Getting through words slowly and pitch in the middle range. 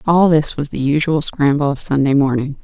No: fast, 205 wpm; medium, 145 Hz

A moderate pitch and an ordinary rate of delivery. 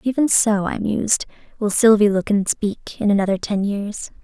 No: high, 210 Hz; average, 185 wpm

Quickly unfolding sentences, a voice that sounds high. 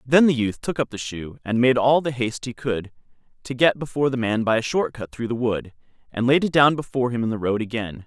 No: fast, 270 wpm; low, 120 Hz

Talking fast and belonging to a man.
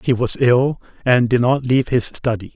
Yes: fast, 210 wpm; male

